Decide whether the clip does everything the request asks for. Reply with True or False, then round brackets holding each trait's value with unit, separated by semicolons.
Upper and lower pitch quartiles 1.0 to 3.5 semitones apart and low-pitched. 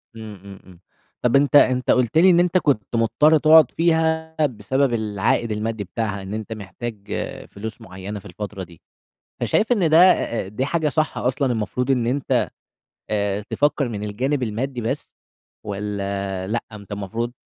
False (5.5 semitones; 115 Hz)